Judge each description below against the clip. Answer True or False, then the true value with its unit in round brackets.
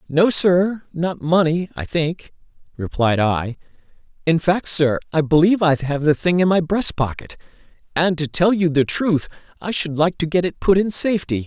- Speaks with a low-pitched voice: False (165 Hz)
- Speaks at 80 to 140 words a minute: False (190 wpm)